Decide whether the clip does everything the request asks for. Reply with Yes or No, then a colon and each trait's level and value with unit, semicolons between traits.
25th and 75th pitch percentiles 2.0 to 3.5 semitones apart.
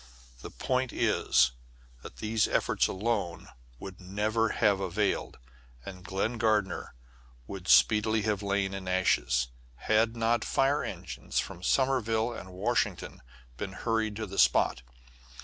Yes: average, 3.2 semitones